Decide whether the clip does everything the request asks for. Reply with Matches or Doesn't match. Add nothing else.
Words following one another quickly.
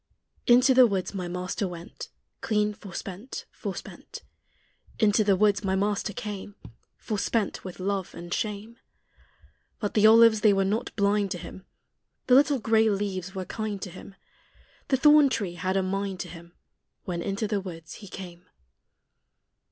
Doesn't match